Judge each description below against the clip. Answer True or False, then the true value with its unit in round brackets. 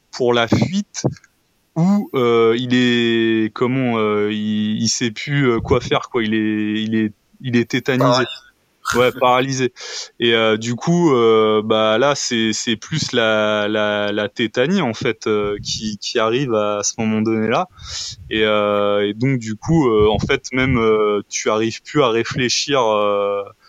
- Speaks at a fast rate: False (170 wpm)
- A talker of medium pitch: False (110 Hz)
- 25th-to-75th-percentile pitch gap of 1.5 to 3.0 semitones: True (2.7 semitones)